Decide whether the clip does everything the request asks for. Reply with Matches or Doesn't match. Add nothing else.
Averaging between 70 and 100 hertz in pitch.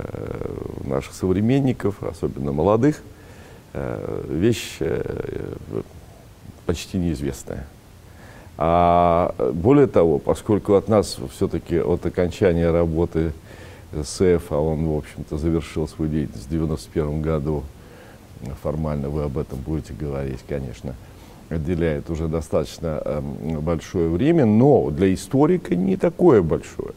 Matches